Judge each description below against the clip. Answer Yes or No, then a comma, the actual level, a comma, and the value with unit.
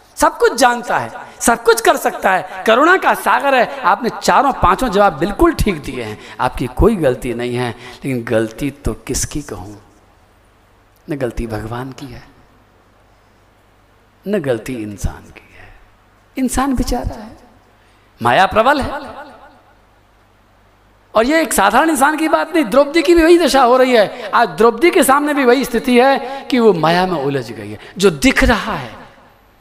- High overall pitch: No, low, 135 Hz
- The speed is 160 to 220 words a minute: Yes, average, 165 wpm